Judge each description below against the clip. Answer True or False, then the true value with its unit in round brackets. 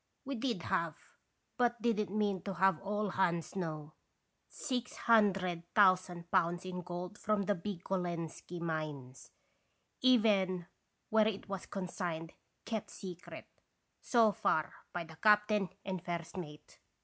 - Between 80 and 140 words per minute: True (135 wpm)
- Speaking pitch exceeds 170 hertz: True (185 Hz)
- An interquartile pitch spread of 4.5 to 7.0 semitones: False (3.5 semitones)